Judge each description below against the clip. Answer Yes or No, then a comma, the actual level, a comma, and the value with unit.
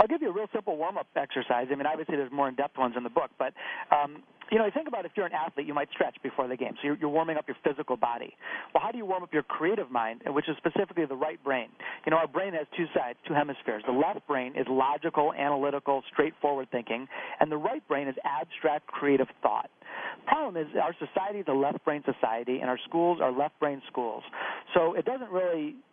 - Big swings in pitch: No, average, 3.6 semitones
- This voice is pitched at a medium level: Yes, medium, 145 Hz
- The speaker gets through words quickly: Yes, fast, 245 wpm